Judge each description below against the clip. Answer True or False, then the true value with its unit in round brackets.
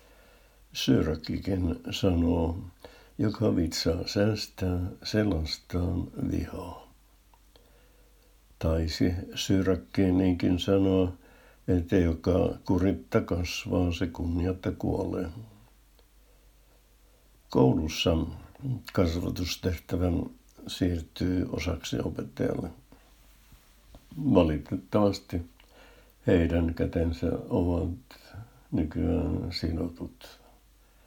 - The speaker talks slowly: True (55 wpm)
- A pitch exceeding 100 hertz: False (90 Hz)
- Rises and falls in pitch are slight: True (2.1 semitones)